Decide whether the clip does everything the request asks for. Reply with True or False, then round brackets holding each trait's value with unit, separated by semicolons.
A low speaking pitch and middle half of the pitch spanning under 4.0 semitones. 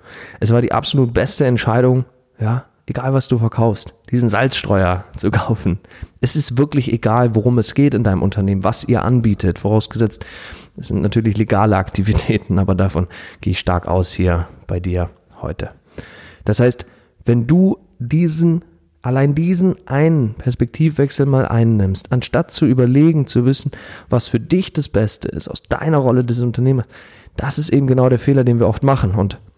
False (120 Hz; 4.7 semitones)